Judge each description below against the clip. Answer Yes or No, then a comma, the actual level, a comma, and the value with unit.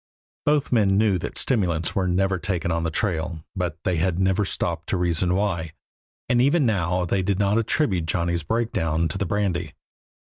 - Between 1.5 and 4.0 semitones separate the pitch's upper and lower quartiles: Yes, average, 3.4 semitones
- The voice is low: Yes, very low, 90 Hz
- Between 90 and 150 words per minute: No, average, 180 wpm